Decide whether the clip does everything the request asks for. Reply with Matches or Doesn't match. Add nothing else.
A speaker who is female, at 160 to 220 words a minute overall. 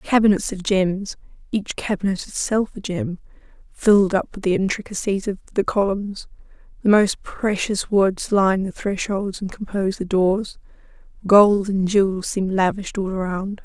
Doesn't match